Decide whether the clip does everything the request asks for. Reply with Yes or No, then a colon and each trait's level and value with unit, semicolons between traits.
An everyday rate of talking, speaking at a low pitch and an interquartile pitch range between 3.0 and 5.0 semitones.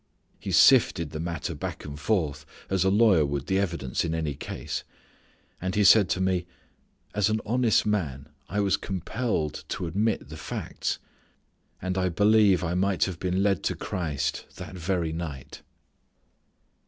Yes: average, 160 wpm; very low, 90 Hz; average, 3.7 semitones